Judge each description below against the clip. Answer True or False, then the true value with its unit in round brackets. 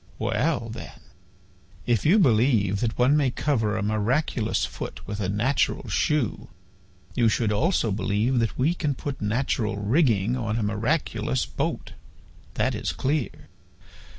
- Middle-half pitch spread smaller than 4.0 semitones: False (4.5 semitones)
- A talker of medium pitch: False (115 Hz)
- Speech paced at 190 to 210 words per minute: False (140 wpm)